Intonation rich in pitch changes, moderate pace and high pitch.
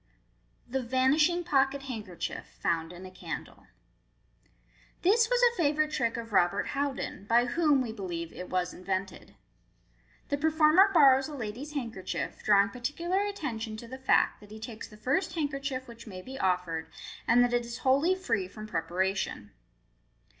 Yes: wide, 6.6 semitones; average, 160 wpm; high, 245 Hz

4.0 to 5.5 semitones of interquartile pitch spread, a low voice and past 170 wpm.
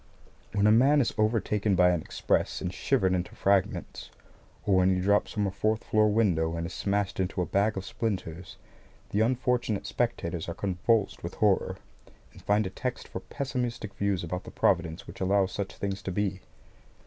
No: average, 2.8 semitones; low, 100 Hz; average, 185 wpm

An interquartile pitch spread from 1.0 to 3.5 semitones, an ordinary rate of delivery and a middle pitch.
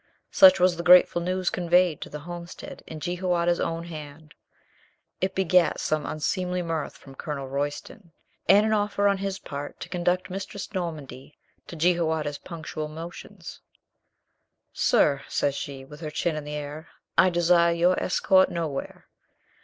Yes: average, 3.1 semitones; average, 155 wpm; medium, 170 Hz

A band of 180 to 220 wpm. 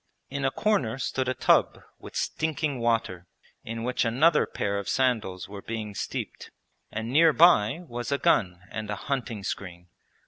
No: average, 165 wpm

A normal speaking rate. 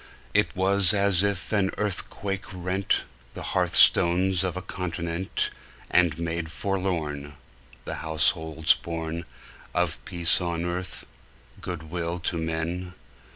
No: slow, 120 wpm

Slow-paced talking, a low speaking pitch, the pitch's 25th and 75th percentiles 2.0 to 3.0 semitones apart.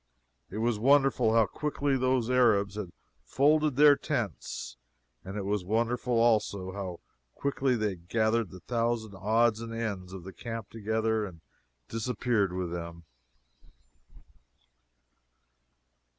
No: slow, 125 wpm; low, 110 Hz; average, 3.5 semitones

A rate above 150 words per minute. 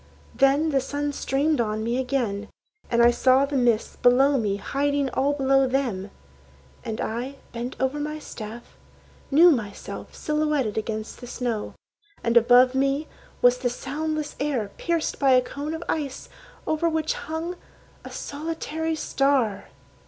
No: average, 145 wpm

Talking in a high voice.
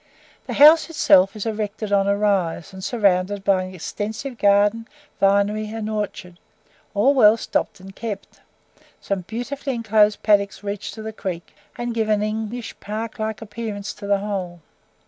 Yes: high, 210 Hz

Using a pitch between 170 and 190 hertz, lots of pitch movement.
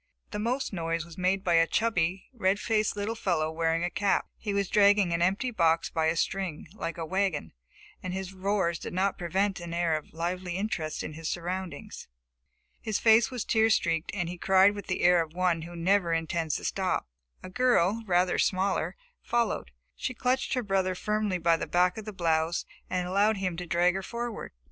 No: medium, 185 Hz; average, 3.3 semitones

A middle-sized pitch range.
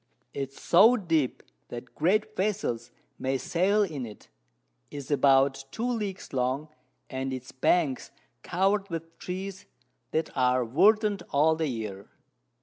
No: wide, 6.8 semitones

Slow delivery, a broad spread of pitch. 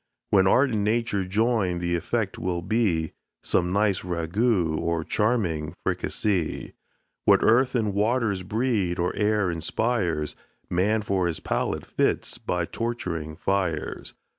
No: slow, 130 wpm; average, 4.2 semitones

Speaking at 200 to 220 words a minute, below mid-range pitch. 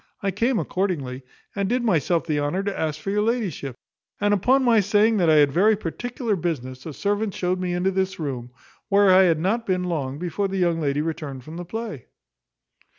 No: fast, 205 wpm; medium, 185 Hz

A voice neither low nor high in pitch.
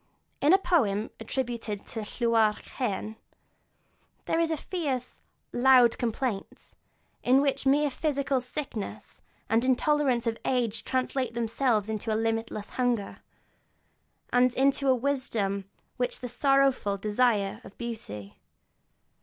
No: high, 245 Hz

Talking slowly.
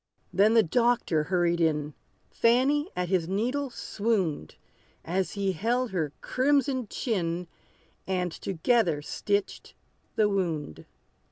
Yes: slow, 110 wpm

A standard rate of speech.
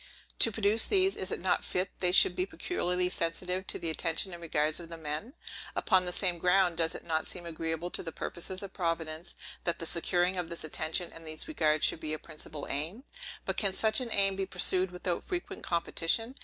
No: fast, 210 wpm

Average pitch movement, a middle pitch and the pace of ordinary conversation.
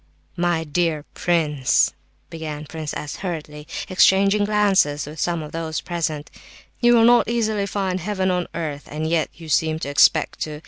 Yes: average, 3.9 semitones; medium, 165 Hz; average, 165 wpm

